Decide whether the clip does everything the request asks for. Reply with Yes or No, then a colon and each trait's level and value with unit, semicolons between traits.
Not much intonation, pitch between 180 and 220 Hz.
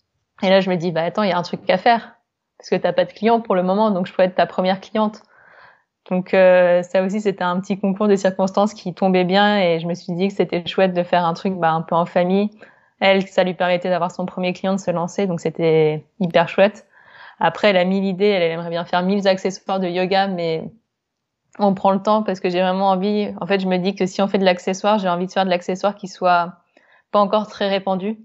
Yes: narrow, 2.2 semitones; high, 190 Hz